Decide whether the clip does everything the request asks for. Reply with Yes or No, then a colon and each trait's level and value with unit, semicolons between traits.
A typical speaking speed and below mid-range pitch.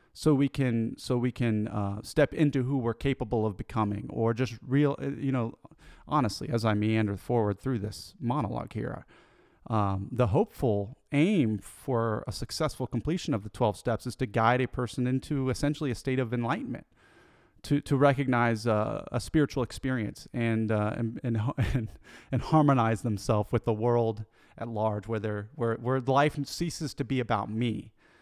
Yes: average, 170 wpm; low, 120 Hz